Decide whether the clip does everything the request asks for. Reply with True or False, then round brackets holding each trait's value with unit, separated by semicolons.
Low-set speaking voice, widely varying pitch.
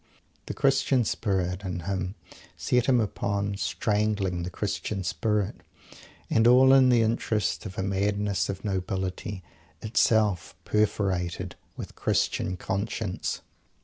False (100 Hz; 2.7 semitones)